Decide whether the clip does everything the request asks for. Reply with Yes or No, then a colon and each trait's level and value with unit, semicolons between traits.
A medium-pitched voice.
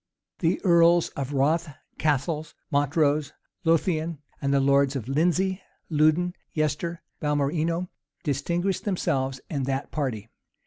Yes: medium, 155 Hz